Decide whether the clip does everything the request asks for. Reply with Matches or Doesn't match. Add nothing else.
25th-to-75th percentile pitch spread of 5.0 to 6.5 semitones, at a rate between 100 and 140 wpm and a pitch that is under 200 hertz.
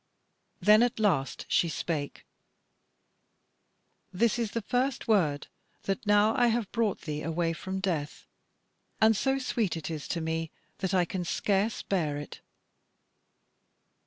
Matches